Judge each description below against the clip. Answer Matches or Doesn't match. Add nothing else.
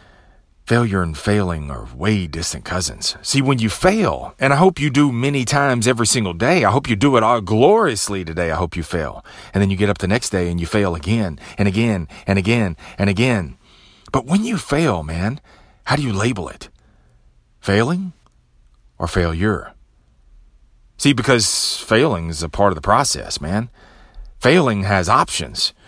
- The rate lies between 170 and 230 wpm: Matches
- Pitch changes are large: Matches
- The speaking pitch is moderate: Doesn't match